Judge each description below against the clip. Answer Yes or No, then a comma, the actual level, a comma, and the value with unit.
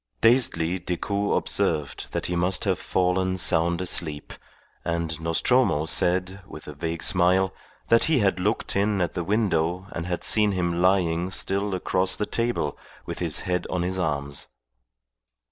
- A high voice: No, very low, 90 Hz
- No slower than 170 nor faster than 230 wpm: No, average, 155 wpm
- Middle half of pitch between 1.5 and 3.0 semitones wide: Yes, narrow, 2.6 semitones